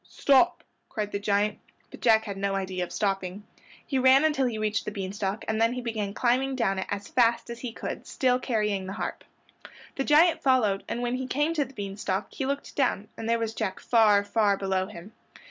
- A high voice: Yes, high, 220 Hz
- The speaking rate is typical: No, fast, 220 wpm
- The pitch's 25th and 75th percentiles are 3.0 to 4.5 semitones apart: Yes, average, 4.1 semitones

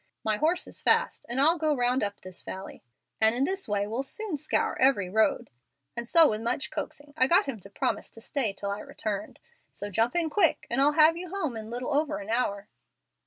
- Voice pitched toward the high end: Yes, high, 245 Hz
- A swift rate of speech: Yes, fast, 220 wpm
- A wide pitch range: Yes, wide, 6.3 semitones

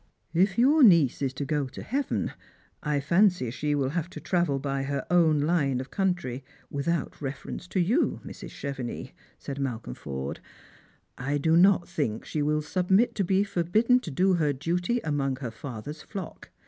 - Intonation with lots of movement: No, average, 4.8 semitones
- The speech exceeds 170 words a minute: Yes, average, 180 wpm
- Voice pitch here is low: No, medium, 150 Hz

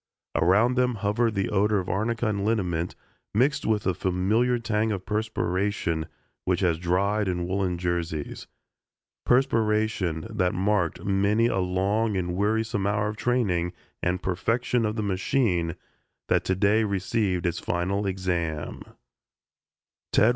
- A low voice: Yes, low, 100 Hz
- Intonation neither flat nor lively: Yes, average, 3.4 semitones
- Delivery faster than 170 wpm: No, slow, 135 wpm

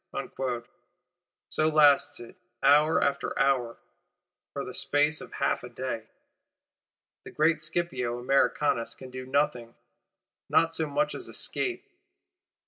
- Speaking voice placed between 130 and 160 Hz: Yes, medium, 140 Hz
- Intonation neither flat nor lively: Yes, average, 3.7 semitones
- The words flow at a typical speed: No, slow, 120 wpm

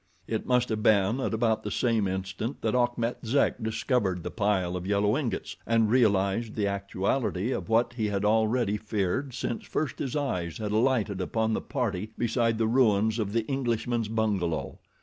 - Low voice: Yes, low, 110 Hz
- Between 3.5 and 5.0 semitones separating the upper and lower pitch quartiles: No, average, 3.0 semitones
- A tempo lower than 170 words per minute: No, average, 175 wpm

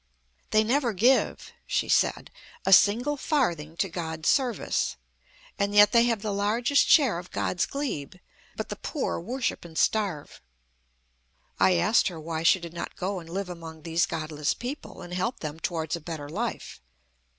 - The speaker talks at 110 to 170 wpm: Yes, average, 165 wpm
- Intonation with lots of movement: Yes, wide, 6.1 semitones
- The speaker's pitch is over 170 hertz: Yes, medium, 185 Hz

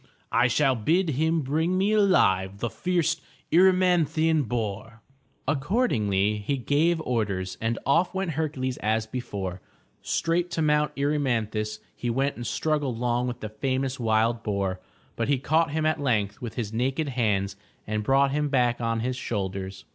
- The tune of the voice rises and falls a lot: Yes, wide, 6.0 semitones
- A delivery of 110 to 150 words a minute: No, average, 165 wpm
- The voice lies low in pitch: Yes, low, 125 Hz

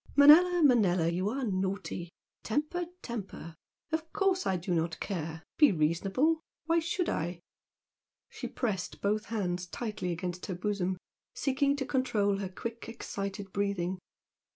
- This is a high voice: Yes, high, 200 Hz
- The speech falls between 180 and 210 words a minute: No, slow, 135 wpm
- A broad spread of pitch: Yes, wide, 7.1 semitones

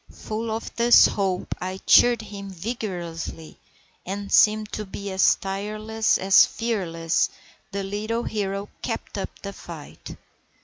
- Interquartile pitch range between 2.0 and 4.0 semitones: Yes, narrow, 2.4 semitones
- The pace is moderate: No, slow, 130 wpm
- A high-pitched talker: Yes, high, 200 Hz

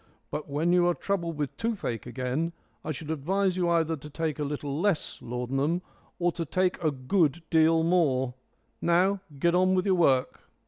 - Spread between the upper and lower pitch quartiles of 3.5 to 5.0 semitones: Yes, average, 3.9 semitones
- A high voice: No, medium, 165 Hz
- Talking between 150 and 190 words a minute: Yes, average, 180 wpm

